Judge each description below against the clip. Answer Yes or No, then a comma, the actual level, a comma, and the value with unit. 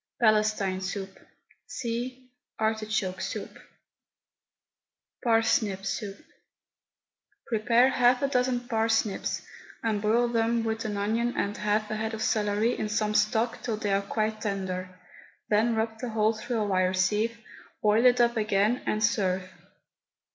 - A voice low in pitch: No, high, 220 Hz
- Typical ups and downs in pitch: No, narrow, 1.9 semitones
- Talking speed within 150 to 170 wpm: No, slow, 135 wpm